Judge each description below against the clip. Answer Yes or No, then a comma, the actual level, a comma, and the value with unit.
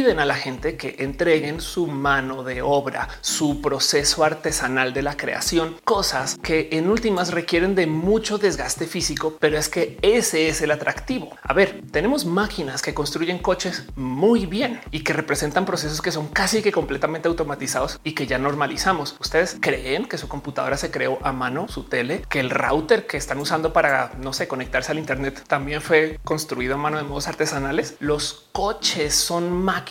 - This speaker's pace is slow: No, average, 180 wpm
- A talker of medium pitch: Yes, medium, 155 Hz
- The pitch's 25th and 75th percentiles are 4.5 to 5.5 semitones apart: No, average, 3.6 semitones